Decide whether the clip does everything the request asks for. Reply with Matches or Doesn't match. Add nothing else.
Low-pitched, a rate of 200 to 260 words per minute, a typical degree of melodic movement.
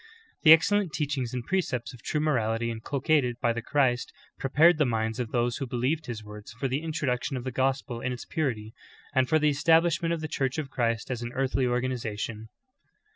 Matches